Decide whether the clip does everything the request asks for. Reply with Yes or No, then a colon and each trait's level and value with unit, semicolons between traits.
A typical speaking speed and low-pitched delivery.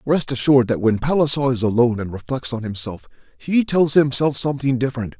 Yes: average, 185 wpm; low, 130 Hz